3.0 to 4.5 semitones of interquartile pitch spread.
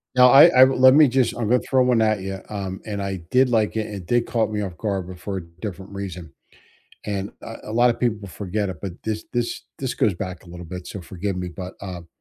Yes: average, 4.1 semitones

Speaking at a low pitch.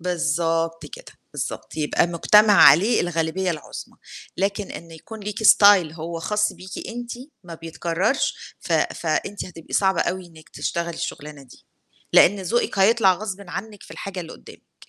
No: medium, 180 Hz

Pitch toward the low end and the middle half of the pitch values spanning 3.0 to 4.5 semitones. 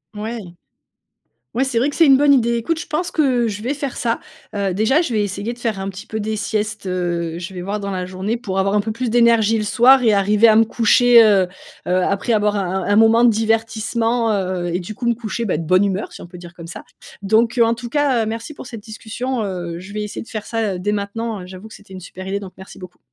No: high, 215 Hz; average, 3.3 semitones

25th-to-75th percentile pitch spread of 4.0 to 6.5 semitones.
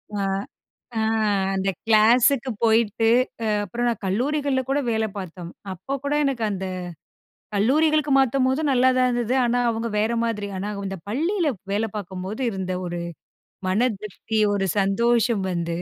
Yes: average, 4.6 semitones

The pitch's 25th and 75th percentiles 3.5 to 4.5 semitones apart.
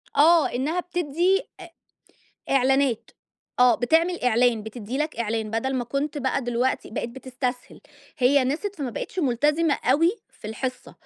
Yes: average, 3.9 semitones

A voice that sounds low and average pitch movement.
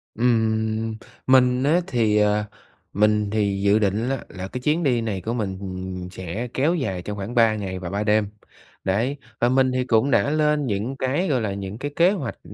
Yes: low, 110 Hz; average, 4.2 semitones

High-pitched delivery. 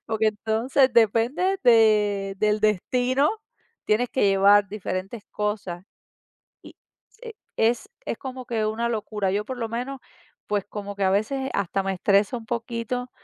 Yes: high, 220 Hz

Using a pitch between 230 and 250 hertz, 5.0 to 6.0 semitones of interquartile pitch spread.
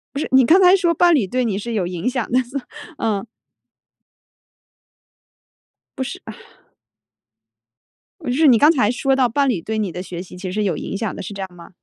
Yes: high, 235 Hz; wide, 5.6 semitones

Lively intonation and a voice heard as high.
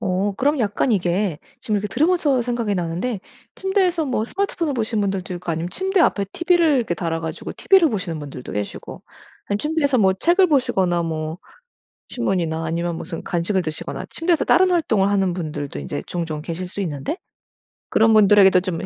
Yes: wide, 8.3 semitones; high, 200 Hz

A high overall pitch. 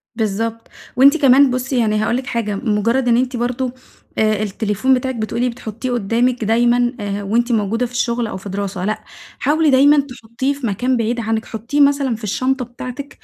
Yes: high, 240 Hz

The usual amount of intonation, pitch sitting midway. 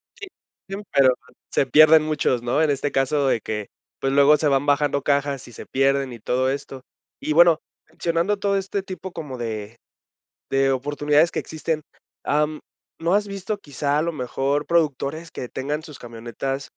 Yes: average, 3.0 semitones; medium, 145 Hz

